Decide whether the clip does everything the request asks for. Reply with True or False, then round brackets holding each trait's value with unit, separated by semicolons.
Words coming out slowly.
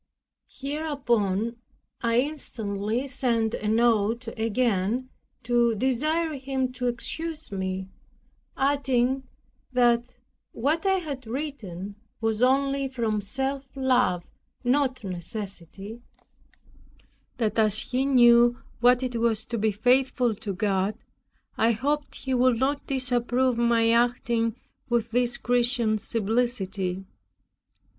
True (105 wpm)